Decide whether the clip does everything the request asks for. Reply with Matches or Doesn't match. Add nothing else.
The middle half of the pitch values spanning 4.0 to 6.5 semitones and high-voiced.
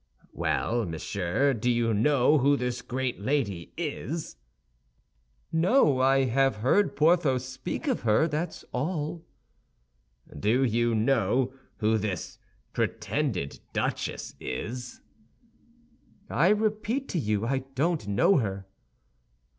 Doesn't match